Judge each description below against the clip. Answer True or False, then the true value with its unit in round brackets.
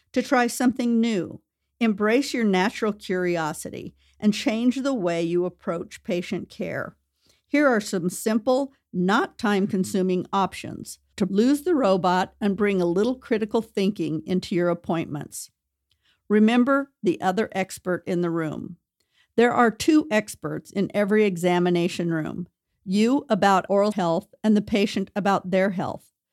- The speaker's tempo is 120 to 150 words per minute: True (140 wpm)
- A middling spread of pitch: True (4.2 semitones)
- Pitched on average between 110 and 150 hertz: False (200 Hz)